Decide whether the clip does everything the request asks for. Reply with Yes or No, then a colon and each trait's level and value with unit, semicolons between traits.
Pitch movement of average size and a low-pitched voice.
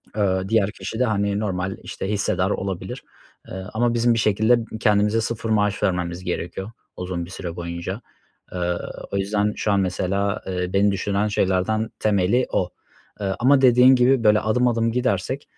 Yes: average, 3.2 semitones; low, 100 Hz